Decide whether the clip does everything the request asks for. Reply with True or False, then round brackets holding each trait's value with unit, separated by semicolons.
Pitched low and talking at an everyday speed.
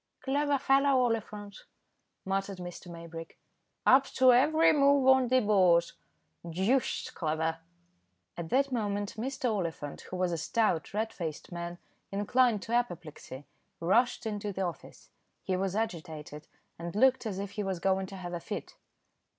False (200 Hz; 150 wpm)